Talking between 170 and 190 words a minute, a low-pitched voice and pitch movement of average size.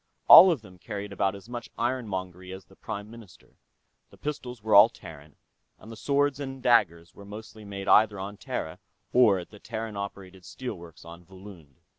Yes: average, 185 wpm; low, 100 Hz; average, 3.9 semitones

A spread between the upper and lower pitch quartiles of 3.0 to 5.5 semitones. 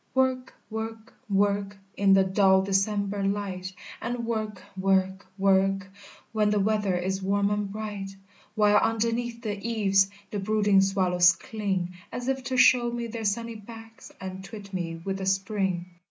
No: narrow, 2.4 semitones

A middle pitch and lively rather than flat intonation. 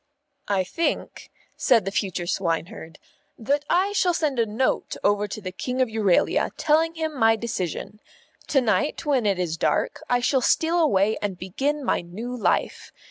No: high, 225 Hz; wide, 6.8 semitones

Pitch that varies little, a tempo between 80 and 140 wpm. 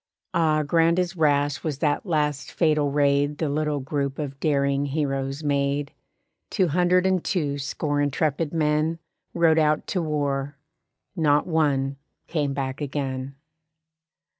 Yes: narrow, 2.2 semitones; slow, 135 wpm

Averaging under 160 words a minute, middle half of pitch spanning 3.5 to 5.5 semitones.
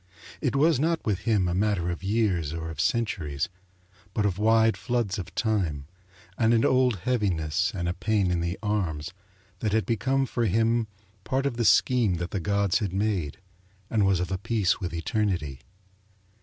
No: average, 180 wpm; average, 4.4 semitones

